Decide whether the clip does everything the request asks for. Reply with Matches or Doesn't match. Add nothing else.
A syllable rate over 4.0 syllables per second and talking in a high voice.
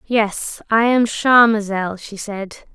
Doesn't match